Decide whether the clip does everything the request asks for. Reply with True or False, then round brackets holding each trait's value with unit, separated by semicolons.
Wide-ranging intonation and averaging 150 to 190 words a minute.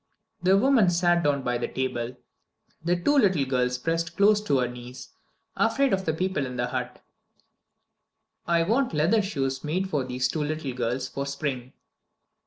True (6.5 semitones; 170 wpm)